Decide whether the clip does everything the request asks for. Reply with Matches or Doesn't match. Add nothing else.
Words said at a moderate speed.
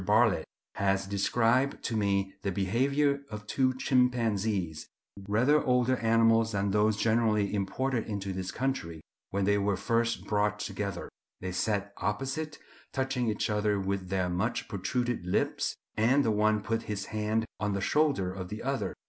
Matches